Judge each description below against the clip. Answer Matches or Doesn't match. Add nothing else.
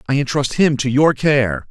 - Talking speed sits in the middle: Doesn't match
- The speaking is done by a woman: Doesn't match